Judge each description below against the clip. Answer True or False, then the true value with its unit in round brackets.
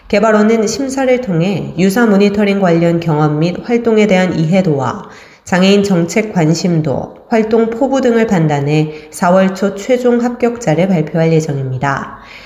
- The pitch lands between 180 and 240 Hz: True (190 Hz)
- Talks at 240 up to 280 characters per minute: False (300 characters per minute)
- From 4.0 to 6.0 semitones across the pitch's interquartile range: True (5.6 semitones)